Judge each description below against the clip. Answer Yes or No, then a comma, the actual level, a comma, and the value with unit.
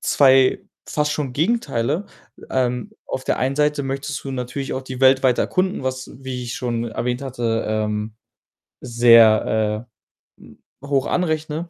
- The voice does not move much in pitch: No, average, 3.1 semitones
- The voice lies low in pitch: Yes, low, 130 Hz